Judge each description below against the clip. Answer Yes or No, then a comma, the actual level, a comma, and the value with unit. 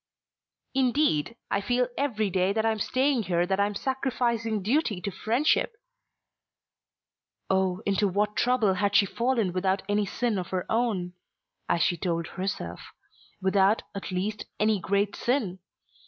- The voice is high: Yes, high, 205 Hz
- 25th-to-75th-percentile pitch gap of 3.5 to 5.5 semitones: Yes, average, 3.8 semitones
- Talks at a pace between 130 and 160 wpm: Yes, average, 150 wpm